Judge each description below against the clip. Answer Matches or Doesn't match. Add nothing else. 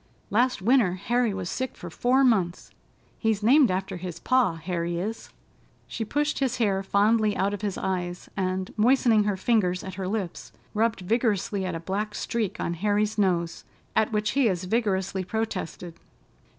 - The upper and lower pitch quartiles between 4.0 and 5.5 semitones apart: Doesn't match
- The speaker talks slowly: Doesn't match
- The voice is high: Matches